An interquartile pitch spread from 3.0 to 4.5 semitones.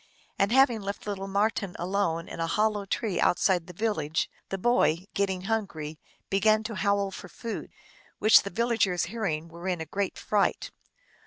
Yes: average, 3.4 semitones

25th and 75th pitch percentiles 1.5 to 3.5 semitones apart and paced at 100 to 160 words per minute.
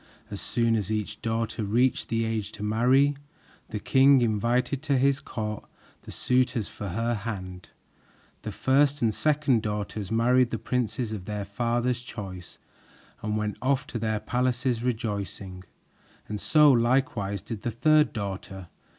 Yes: average, 3.2 semitones; average, 150 wpm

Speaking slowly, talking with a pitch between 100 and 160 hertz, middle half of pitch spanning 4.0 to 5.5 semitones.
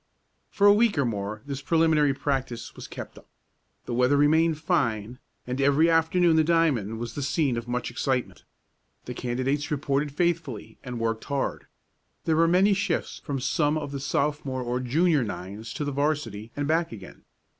No: average, 175 wpm; medium, 140 Hz; average, 4.6 semitones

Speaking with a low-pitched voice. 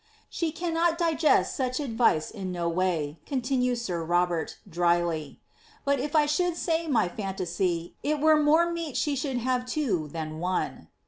No: very high, 250 Hz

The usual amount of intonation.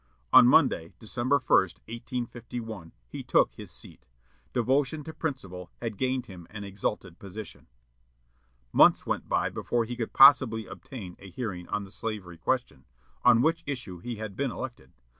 Yes: average, 5.0 semitones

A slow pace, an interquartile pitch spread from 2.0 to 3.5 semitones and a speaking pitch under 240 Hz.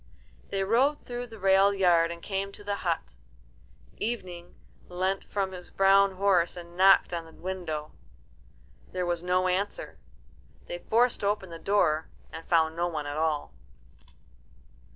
No: average, 150 wpm; average, 2.7 semitones; medium, 185 Hz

